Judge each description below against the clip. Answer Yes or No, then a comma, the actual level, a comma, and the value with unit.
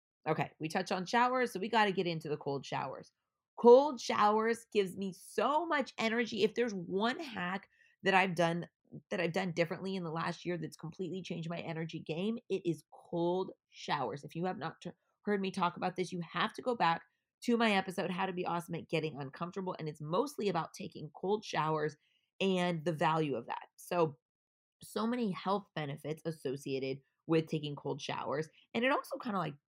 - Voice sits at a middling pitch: Yes, medium, 180 Hz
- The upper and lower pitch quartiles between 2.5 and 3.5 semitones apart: No, average, 4.3 semitones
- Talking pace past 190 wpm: Yes, average, 200 wpm